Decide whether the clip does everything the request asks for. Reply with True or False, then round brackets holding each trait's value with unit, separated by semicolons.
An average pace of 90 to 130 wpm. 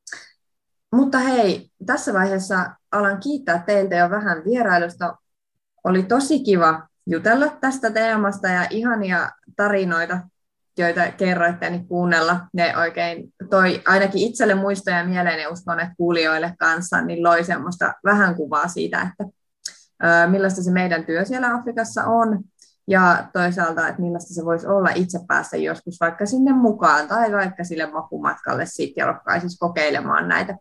False (140 wpm)